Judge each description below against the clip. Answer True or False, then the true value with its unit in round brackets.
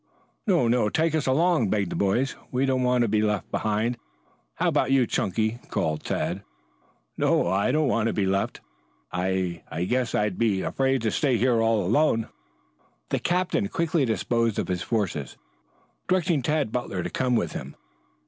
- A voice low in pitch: True (115 Hz)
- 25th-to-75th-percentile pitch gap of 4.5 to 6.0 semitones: True (4.8 semitones)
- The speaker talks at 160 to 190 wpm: True (175 wpm)